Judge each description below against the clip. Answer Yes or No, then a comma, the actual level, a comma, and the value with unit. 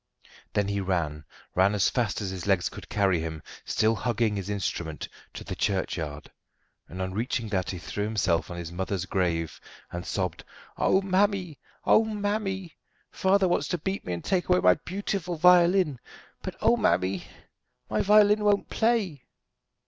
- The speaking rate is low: No, average, 160 wpm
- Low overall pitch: Yes, low, 105 Hz